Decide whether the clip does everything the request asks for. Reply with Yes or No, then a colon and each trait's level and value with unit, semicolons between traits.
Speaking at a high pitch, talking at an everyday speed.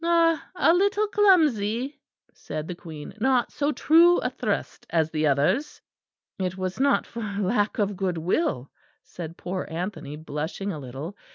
Yes: high, 200 Hz; average, 155 wpm